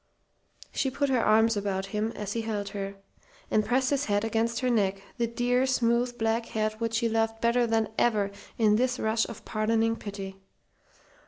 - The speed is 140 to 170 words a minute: No, average, 180 wpm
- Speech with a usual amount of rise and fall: No, narrow, 2.0 semitones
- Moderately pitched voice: No, high, 225 Hz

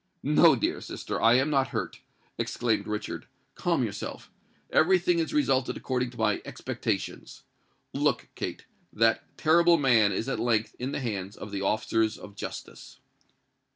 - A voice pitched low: Yes, low, 120 Hz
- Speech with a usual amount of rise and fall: Yes, average, 4.5 semitones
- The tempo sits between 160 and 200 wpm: No, average, 145 wpm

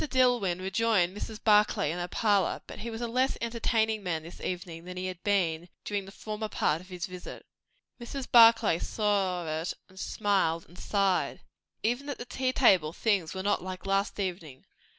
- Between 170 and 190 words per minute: Yes, average, 185 wpm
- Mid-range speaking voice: No, high, 195 Hz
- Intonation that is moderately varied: Yes, average, 3.8 semitones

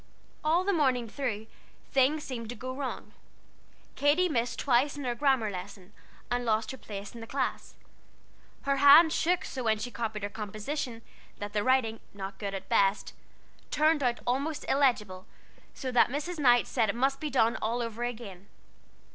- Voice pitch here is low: No, high, 245 Hz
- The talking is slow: No, average, 170 wpm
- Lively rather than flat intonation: No, average, 4.4 semitones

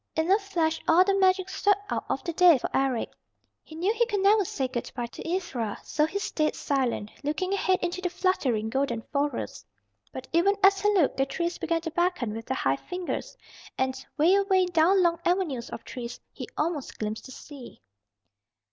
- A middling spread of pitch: No, wide, 6.1 semitones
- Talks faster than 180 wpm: Yes, average, 195 wpm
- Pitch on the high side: Yes, very high, 330 Hz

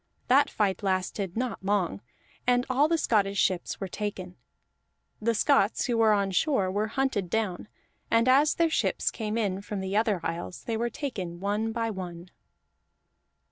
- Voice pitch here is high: Yes, high, 210 Hz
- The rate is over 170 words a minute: No, average, 165 wpm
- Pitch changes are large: No, average, 3.8 semitones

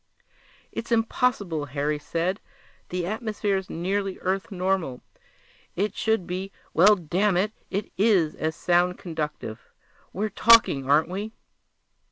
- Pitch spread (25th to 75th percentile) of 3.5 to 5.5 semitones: Yes, average, 4.0 semitones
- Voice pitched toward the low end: No, medium, 185 Hz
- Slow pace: Yes, slow, 120 wpm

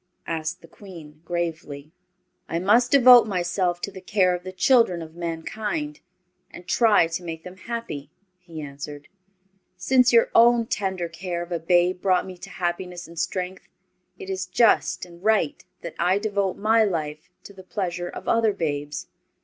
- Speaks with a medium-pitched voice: Yes, medium, 180 Hz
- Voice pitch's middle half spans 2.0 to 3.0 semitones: No, average, 3.8 semitones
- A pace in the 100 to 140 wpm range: No, average, 165 wpm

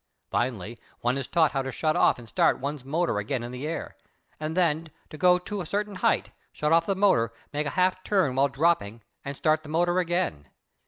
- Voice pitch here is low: No, medium, 155 Hz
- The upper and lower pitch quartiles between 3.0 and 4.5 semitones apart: No, average, 5.1 semitones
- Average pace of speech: No, fast, 215 wpm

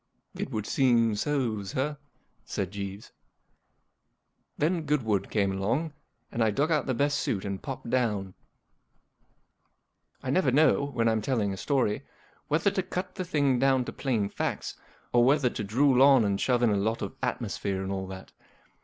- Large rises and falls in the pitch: Yes, wide, 5.7 semitones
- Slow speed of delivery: No, average, 170 wpm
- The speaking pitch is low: Yes, low, 120 Hz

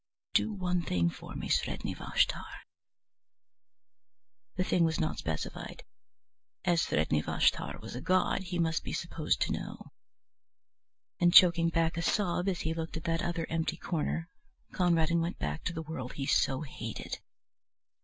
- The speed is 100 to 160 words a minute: Yes, average, 155 wpm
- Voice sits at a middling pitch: Yes, medium, 165 Hz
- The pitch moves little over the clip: Yes, narrow, 1.9 semitones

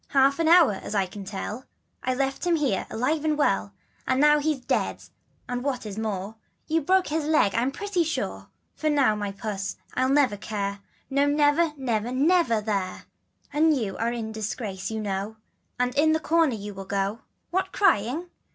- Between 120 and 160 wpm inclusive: No, average, 185 wpm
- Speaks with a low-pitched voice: No, very high, 255 Hz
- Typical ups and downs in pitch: No, wide, 6.4 semitones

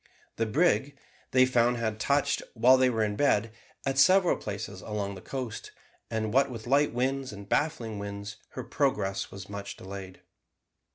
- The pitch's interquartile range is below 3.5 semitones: No, average, 4.8 semitones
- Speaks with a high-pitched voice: No, low, 115 Hz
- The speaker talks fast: No, average, 165 wpm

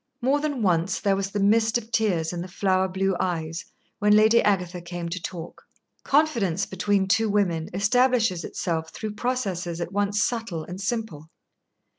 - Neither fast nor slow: Yes, average, 165 wpm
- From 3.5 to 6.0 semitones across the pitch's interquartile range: Yes, average, 3.9 semitones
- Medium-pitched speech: No, high, 195 Hz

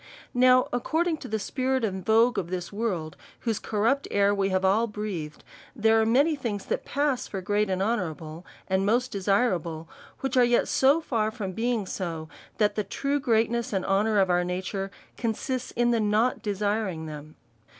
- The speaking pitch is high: Yes, high, 210 Hz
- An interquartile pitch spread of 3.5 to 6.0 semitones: Yes, average, 4.2 semitones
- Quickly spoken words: No, average, 180 wpm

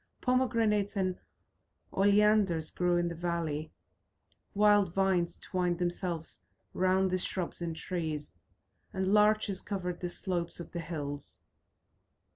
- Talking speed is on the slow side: Yes, slow, 115 wpm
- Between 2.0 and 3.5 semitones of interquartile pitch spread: Yes, average, 2.7 semitones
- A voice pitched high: No, medium, 180 Hz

